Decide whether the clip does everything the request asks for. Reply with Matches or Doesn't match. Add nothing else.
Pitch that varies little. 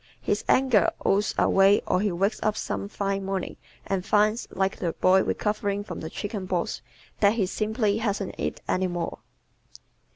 Matches